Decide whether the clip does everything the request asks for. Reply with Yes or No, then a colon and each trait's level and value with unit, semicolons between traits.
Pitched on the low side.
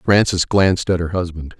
Yes: very low, 90 Hz